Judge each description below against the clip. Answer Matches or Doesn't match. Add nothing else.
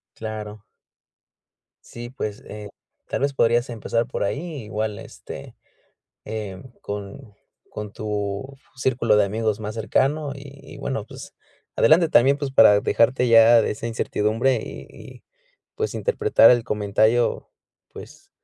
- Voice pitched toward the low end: Matches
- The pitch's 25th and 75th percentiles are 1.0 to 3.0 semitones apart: Doesn't match